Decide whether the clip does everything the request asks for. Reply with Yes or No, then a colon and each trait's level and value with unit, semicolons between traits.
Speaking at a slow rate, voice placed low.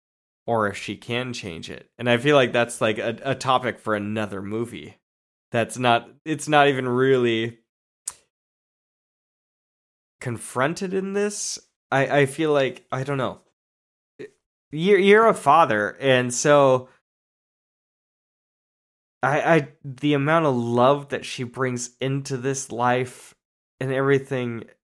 Yes: slow, 130 wpm; low, 130 Hz